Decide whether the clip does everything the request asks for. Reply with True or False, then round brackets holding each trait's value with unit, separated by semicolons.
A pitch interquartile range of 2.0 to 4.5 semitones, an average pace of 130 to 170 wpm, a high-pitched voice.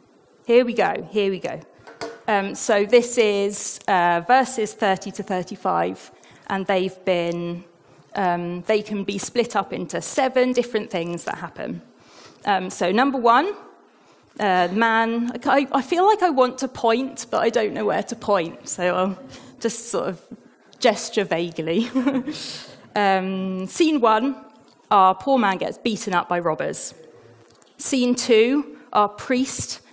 False (5.0 semitones; 145 wpm; 215 Hz)